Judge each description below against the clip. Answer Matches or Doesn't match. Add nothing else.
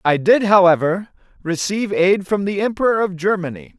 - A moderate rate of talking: Matches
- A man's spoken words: Matches